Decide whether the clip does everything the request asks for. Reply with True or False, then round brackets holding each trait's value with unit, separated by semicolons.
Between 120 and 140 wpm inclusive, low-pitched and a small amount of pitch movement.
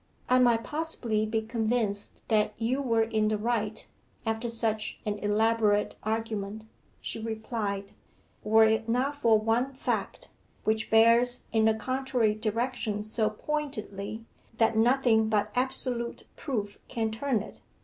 False (135 wpm; 225 Hz; 1.9 semitones)